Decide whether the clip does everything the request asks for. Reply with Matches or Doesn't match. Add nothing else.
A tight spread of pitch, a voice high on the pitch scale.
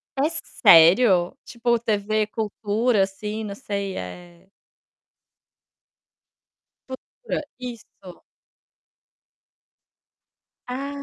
Doesn't match